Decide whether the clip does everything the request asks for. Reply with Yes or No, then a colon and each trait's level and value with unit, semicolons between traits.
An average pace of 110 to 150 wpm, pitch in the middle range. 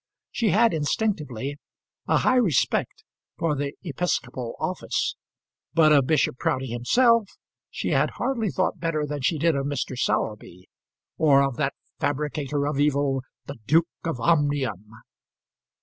Yes: slow, 135 wpm; medium, 145 Hz